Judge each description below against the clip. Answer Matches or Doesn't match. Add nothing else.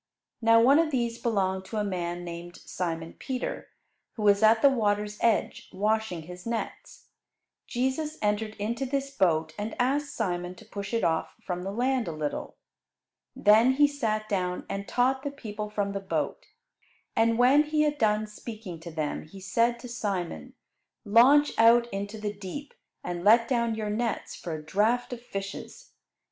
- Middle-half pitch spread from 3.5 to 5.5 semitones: Matches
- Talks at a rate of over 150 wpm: Matches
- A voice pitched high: Matches